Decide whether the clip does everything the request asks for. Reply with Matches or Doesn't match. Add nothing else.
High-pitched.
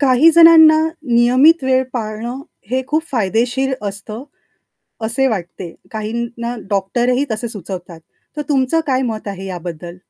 Matches